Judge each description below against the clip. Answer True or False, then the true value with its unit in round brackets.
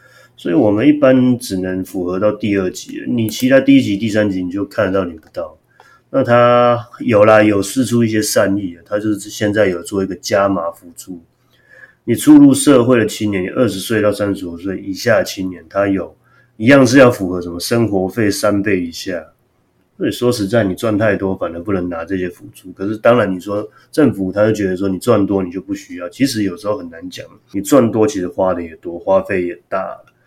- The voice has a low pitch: True (100 Hz)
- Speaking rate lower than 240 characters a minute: False (305 characters per minute)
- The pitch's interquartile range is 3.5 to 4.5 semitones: True (3.8 semitones)